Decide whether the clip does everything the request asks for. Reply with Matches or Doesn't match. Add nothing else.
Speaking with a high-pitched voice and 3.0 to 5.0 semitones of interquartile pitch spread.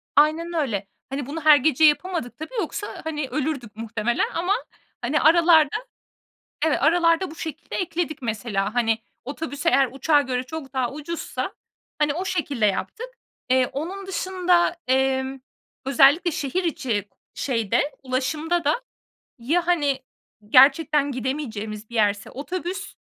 Matches